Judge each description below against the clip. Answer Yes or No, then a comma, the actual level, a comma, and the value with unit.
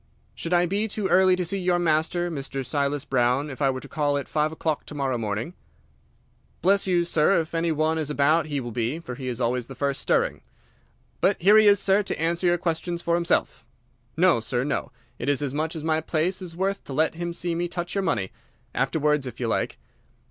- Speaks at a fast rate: Yes, fast, 225 wpm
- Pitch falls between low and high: Yes, medium, 160 Hz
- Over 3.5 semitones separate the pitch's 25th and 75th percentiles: Yes, average, 4.0 semitones